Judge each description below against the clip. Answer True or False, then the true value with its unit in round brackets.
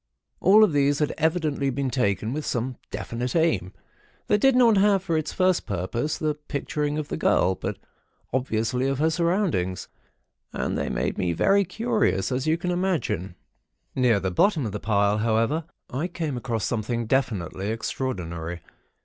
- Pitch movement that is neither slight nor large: False (7.3 semitones)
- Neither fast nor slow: True (165 wpm)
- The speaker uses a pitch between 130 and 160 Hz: True (135 Hz)